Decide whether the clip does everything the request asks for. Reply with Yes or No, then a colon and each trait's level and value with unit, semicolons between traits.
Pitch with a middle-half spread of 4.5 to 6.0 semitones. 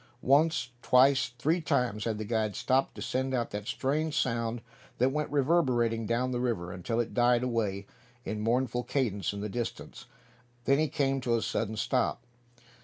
No: average, 2.9 semitones